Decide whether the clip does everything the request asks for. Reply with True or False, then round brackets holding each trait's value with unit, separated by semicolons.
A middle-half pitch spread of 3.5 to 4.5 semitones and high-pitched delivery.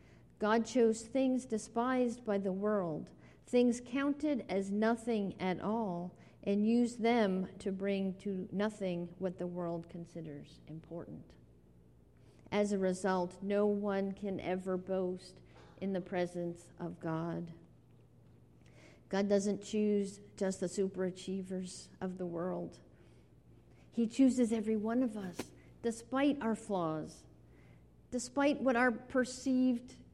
True (4.2 semitones; 200 Hz)